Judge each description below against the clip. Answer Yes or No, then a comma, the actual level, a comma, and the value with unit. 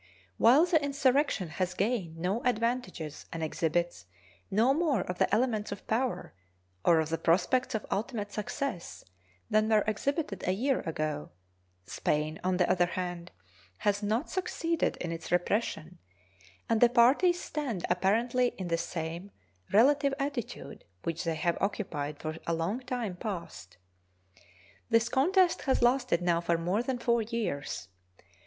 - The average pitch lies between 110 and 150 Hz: No, high, 210 Hz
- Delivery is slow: No, average, 145 wpm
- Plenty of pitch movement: Yes, wide, 6.6 semitones